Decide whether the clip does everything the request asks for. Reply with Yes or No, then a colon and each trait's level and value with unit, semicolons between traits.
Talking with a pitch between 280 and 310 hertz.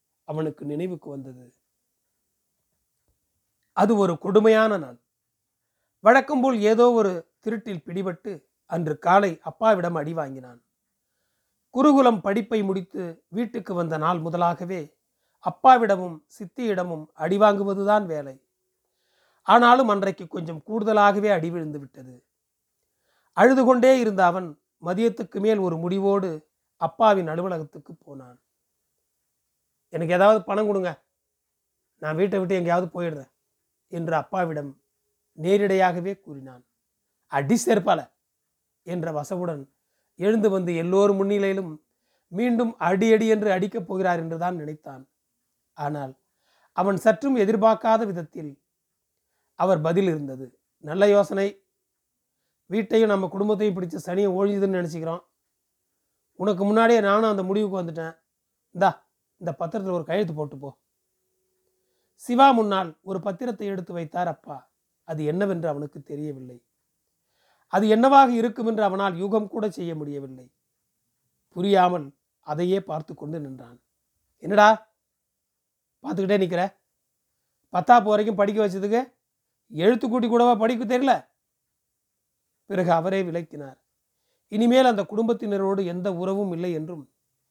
No: medium, 185 Hz